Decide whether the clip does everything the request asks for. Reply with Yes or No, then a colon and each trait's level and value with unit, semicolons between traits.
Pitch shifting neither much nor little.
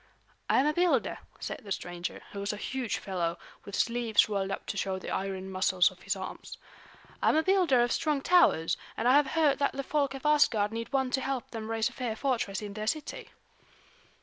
No: wide, 5.9 semitones